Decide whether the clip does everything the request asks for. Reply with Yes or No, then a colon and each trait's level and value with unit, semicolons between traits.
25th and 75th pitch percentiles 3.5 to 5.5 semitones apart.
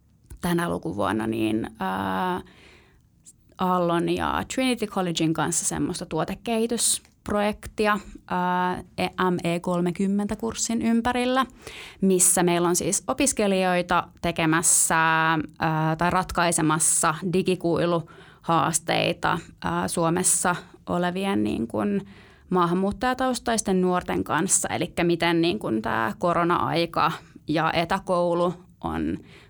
No: narrow, 2.6 semitones